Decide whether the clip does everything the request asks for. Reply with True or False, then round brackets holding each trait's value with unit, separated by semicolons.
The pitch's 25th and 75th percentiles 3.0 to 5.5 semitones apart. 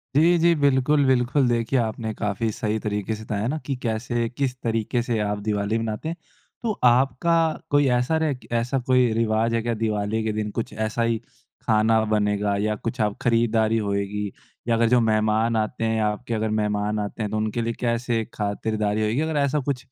False (2.5 semitones)